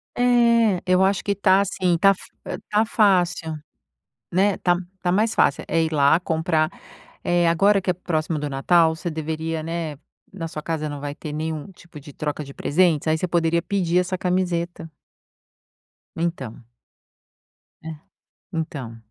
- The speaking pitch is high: No, medium, 170 Hz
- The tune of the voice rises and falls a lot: No, average, 2.8 semitones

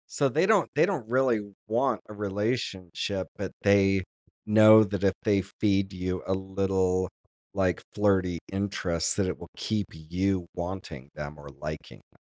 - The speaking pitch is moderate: No, very low, 95 Hz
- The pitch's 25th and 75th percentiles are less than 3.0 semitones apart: Yes, narrow, 2.6 semitones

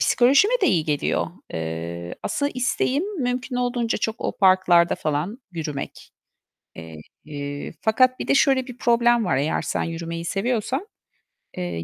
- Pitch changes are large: Yes, wide, 8.2 semitones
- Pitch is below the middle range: No, high, 215 Hz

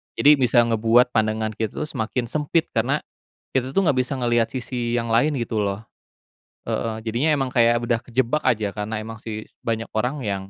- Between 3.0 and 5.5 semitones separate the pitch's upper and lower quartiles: No, narrow, 2.6 semitones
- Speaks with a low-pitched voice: Yes, low, 120 Hz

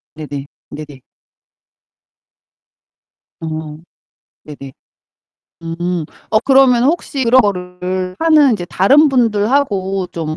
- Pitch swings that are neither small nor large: No, wide, 7.9 semitones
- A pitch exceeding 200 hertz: No, medium, 185 Hz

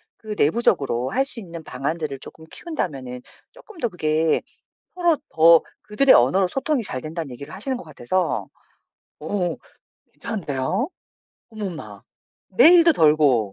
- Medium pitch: Yes, medium, 165 Hz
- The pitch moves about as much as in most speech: No, wide, 8.4 semitones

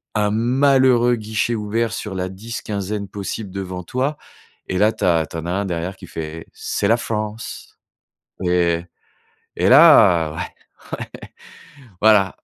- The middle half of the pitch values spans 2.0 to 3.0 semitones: No, average, 3.9 semitones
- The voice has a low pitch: Yes, low, 105 Hz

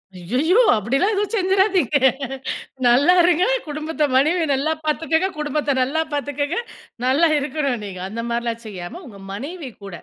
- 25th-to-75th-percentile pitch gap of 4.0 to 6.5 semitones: Yes, wide, 5.5 semitones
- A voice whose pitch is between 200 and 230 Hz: No, very high, 290 Hz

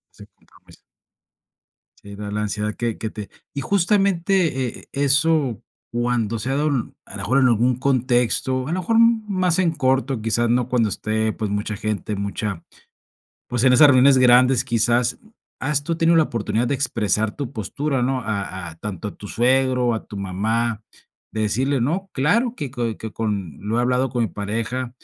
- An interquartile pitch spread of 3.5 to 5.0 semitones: Yes, average, 4.3 semitones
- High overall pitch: No, low, 120 Hz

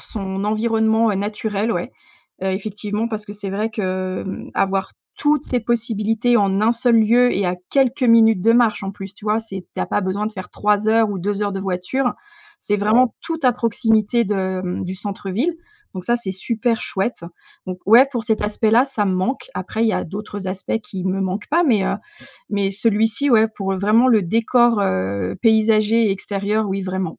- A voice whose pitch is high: Yes, high, 210 Hz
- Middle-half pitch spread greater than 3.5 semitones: No, average, 2.8 semitones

